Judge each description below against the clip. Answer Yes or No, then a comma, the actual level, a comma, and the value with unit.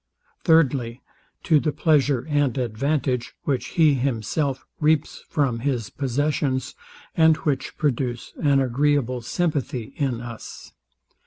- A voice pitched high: No, low, 135 Hz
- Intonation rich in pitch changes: No, average, 3.2 semitones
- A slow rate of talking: Yes, slow, 110 wpm